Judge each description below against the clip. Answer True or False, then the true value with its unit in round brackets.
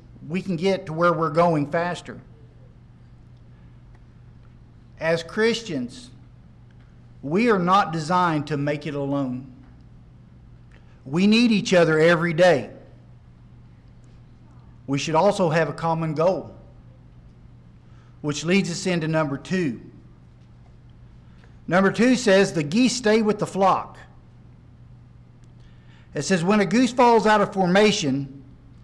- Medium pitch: True (160 Hz)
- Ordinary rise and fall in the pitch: False (7.5 semitones)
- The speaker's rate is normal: False (115 wpm)